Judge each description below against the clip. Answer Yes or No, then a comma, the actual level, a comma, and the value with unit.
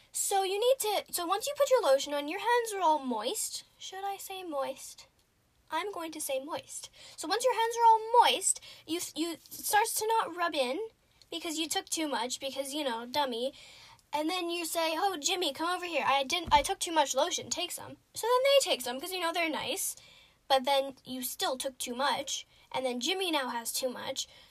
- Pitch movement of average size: No, wide, 6.0 semitones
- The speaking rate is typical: No, fast, 220 wpm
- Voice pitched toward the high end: Yes, very high, 325 Hz